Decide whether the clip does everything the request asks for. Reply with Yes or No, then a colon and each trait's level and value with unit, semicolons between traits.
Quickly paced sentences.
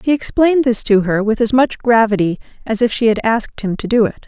Yes: fast, 250 wpm